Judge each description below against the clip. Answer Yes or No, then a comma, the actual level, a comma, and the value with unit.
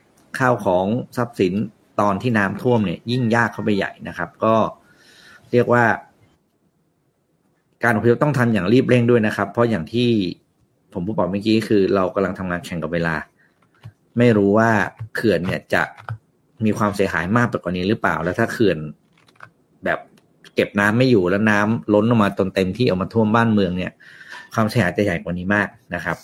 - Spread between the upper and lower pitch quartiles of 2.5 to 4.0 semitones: Yes, average, 3.4 semitones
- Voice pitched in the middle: No, low, 105 Hz